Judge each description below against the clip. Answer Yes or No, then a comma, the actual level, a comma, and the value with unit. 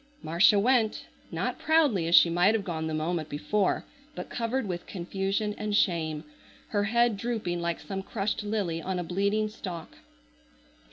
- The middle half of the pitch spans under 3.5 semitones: No, average, 3.9 semitones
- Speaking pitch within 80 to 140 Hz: No, high, 195 Hz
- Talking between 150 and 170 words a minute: Yes, average, 160 wpm